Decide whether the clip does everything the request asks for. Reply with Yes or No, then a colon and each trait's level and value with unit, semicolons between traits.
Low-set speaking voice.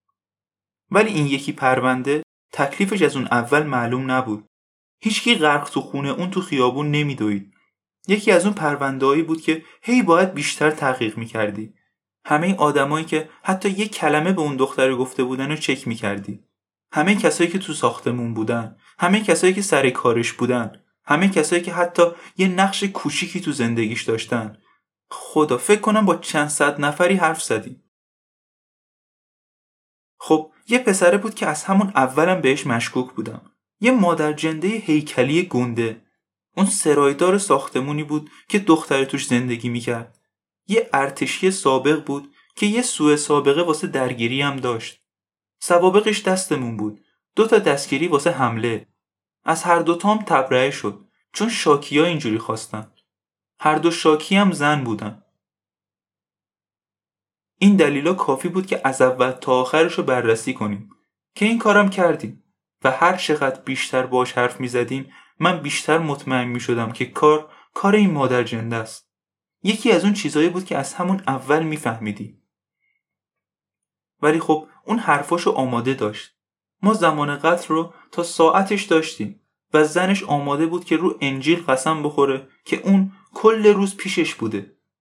No: medium, 150 Hz